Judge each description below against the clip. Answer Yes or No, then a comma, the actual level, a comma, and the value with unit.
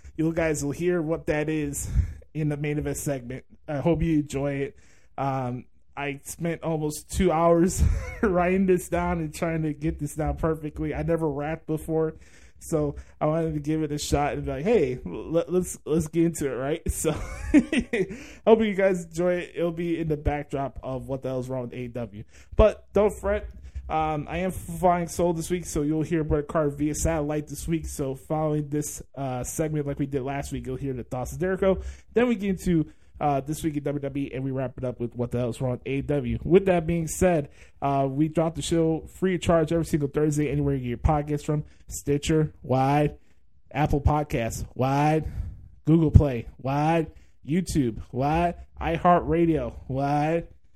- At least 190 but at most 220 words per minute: Yes, average, 195 wpm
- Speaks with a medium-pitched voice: Yes, medium, 150 Hz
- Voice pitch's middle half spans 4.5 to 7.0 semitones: No, average, 3.4 semitones